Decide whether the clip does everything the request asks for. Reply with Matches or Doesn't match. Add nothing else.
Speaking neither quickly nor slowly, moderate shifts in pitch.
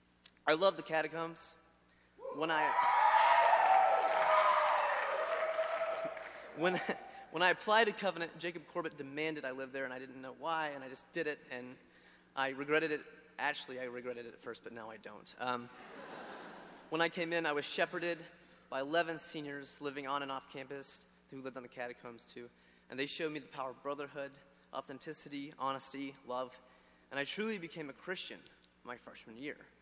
Matches